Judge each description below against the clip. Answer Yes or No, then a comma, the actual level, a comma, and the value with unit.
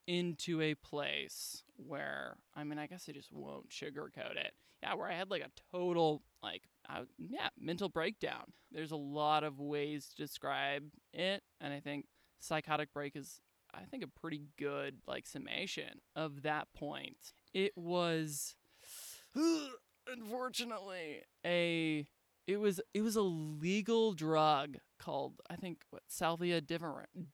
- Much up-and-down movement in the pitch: No, average, 3.5 semitones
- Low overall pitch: No, medium, 160 Hz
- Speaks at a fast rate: No, average, 145 wpm